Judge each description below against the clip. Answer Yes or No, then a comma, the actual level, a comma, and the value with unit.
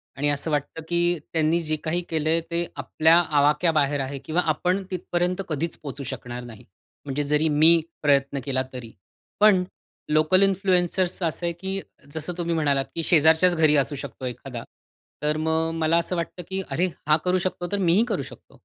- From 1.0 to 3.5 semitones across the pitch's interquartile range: Yes, average, 3.2 semitones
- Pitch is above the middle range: No, medium, 160 Hz